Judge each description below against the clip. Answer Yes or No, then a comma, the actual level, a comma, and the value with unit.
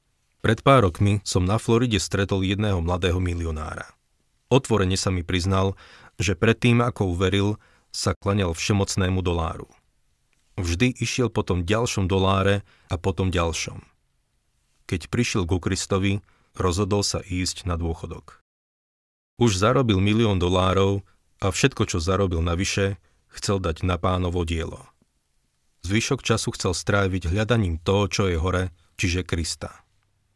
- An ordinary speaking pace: Yes, average, 130 wpm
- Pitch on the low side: Yes, very low, 95 Hz